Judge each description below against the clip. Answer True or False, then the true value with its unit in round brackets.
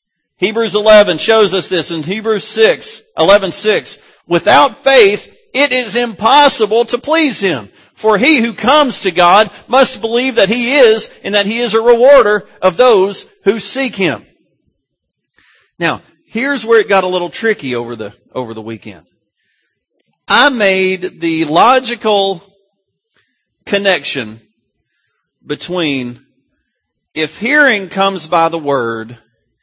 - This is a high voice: True (200 Hz)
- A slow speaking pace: True (130 wpm)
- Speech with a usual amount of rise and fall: False (6.1 semitones)